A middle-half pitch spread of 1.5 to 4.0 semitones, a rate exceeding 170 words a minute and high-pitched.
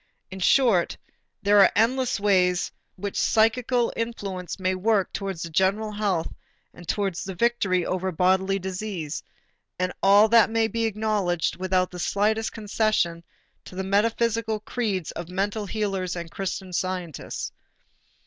No: average, 3.0 semitones; average, 140 wpm; high, 195 Hz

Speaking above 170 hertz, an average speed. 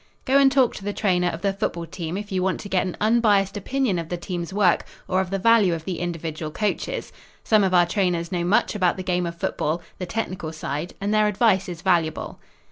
No: medium, 185 Hz; fast, 230 wpm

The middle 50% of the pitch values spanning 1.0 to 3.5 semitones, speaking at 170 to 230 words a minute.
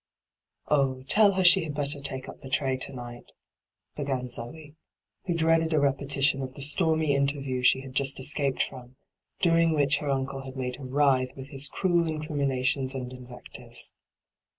Yes: narrow, 2.4 semitones; average, 175 wpm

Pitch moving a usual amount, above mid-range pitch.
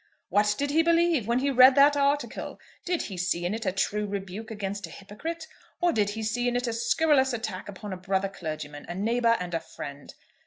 No: wide, 5.7 semitones; high, 220 Hz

